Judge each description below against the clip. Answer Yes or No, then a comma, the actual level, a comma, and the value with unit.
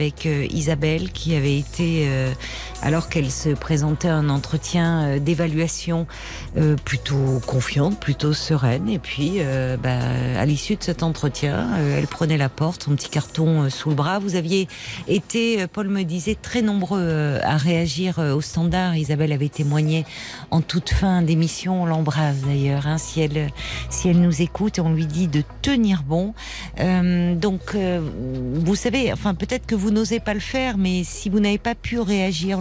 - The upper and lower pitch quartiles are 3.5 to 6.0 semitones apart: Yes, average, 4.2 semitones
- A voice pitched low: No, medium, 160 Hz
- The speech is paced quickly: No, average, 165 wpm